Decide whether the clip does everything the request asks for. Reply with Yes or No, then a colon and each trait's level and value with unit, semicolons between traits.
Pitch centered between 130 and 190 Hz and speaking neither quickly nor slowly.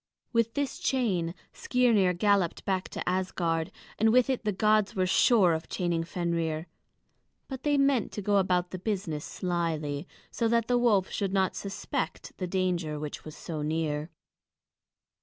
Yes: medium, 185 Hz; average, 160 wpm